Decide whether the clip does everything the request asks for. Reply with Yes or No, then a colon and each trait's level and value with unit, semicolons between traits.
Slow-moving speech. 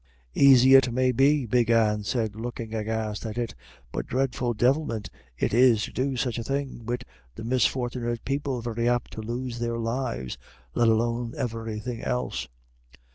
No: average, 160 wpm